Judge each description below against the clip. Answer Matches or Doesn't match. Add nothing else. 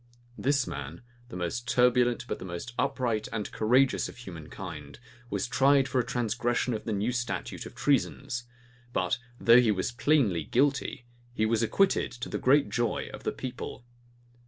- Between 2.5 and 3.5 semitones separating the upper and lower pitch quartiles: Matches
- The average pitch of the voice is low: Matches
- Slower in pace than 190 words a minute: Matches